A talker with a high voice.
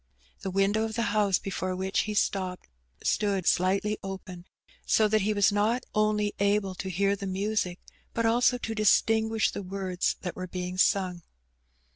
Yes: high, 200 Hz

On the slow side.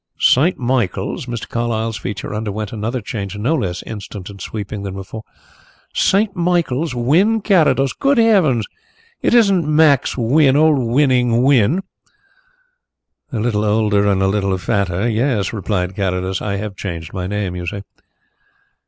No: average, 145 wpm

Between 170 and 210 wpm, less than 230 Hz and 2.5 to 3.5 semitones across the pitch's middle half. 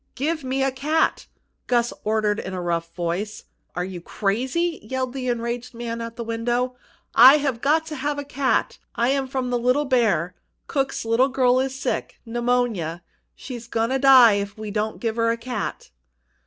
No: average, 175 wpm; high, 240 Hz; average, 3.2 semitones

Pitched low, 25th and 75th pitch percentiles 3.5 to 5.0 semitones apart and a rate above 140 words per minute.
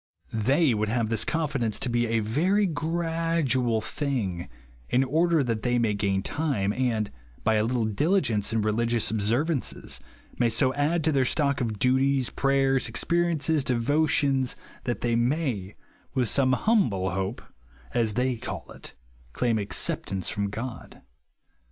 Yes: low, 125 Hz; average, 4.7 semitones; average, 150 wpm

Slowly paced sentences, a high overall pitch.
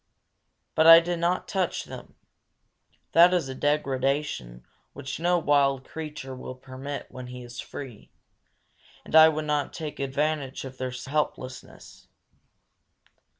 No: slow, 130 wpm; medium, 140 Hz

